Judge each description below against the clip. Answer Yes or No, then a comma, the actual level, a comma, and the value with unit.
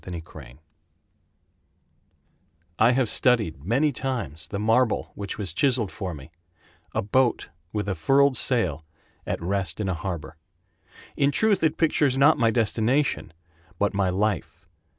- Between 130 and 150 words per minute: Yes, average, 140 wpm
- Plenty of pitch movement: Yes, wide, 6.1 semitones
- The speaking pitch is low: Yes, low, 110 Hz